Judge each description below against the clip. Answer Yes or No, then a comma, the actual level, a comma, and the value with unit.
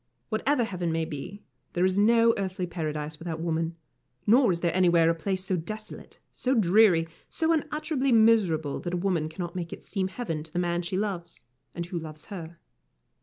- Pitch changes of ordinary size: Yes, average, 4.4 semitones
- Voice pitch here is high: No, medium, 180 Hz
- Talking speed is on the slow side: No, average, 185 wpm